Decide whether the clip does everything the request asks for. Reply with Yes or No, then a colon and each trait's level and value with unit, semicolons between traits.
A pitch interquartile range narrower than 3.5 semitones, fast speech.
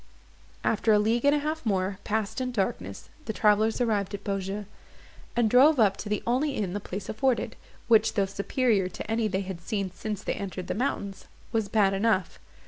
No: average, 2.9 semitones; average, 195 wpm